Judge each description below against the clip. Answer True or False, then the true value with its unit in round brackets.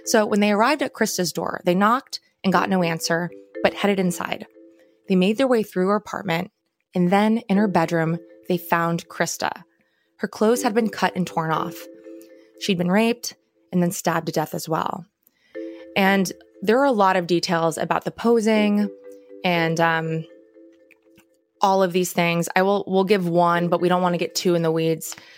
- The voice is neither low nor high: True (175 Hz)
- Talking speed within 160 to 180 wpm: False (190 wpm)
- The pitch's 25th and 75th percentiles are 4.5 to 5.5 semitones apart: False (3.7 semitones)